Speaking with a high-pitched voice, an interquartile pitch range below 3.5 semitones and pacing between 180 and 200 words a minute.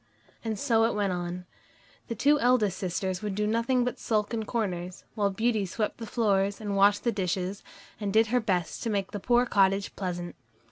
Yes: high, 205 Hz; average, 3.1 semitones; average, 195 wpm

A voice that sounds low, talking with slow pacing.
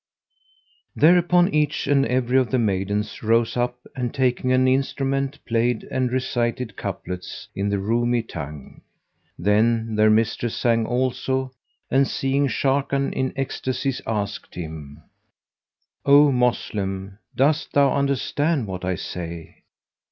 Yes: low, 125 Hz; slow, 120 wpm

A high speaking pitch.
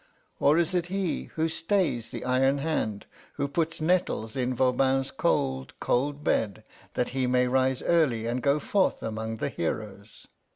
No: low, 135 Hz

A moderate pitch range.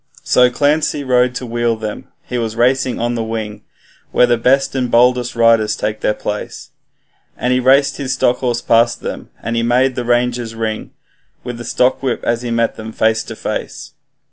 No: narrow, 1.6 semitones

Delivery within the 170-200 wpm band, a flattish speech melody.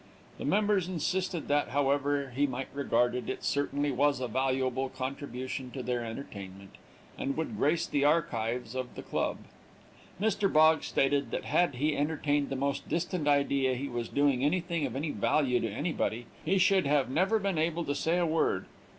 No: average, 175 wpm; average, 3.7 semitones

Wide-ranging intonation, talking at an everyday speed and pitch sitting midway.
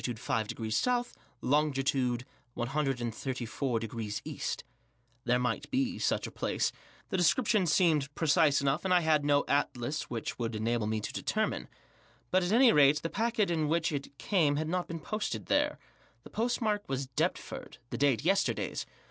Yes: wide, 6.1 semitones; average, 155 wpm; medium, 145 Hz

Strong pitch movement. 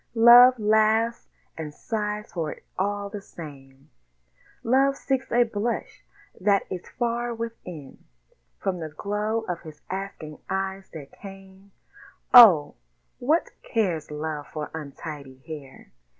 Yes: wide, 6.4 semitones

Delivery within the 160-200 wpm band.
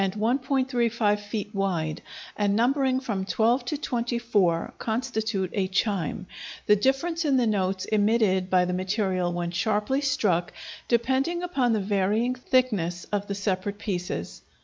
No: slow, 135 wpm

